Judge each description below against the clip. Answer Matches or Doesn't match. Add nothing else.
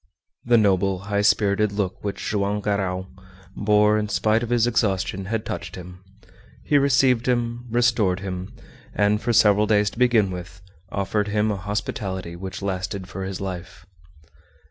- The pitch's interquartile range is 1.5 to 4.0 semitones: Matches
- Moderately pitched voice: Doesn't match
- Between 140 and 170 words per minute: Matches